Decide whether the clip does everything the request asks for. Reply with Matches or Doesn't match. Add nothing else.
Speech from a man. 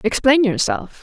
Doesn't match